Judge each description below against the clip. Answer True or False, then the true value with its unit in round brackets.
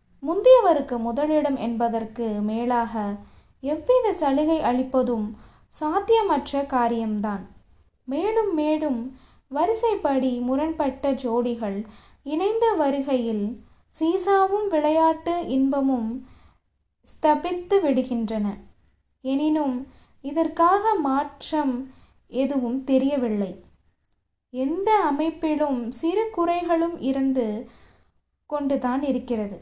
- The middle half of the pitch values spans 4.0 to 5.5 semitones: True (5.0 semitones)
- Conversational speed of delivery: False (65 wpm)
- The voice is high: True (275 Hz)